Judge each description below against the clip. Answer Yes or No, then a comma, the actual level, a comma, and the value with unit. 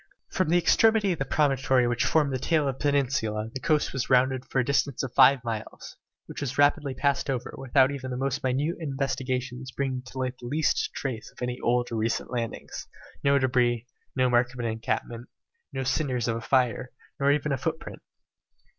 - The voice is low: Yes, low, 130 Hz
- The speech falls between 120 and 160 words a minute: No, average, 200 wpm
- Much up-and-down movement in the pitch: No, narrow, 2.4 semitones